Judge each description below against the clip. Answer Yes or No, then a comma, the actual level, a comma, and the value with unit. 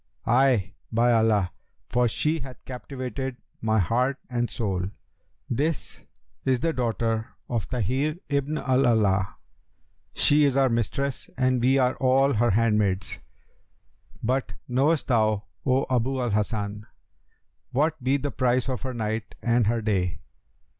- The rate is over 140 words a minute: No, slow, 135 wpm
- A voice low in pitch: Yes, low, 125 Hz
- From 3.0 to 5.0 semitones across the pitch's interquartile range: Yes, average, 3.3 semitones